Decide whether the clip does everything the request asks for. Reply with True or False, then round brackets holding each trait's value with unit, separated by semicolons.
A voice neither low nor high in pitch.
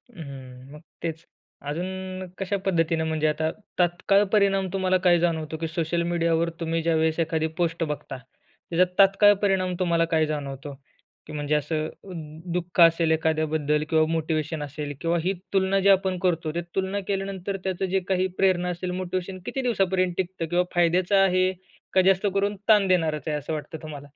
True (170 Hz)